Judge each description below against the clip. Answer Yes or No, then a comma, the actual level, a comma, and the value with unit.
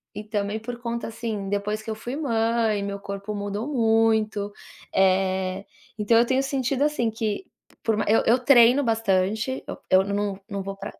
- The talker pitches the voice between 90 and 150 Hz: No, high, 220 Hz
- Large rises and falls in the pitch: No, average, 2.7 semitones